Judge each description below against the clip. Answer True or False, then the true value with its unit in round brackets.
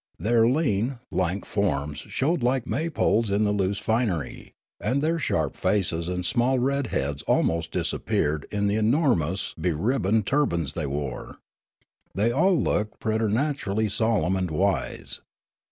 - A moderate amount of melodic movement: False (5.8 semitones)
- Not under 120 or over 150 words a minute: True (140 wpm)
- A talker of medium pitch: False (105 Hz)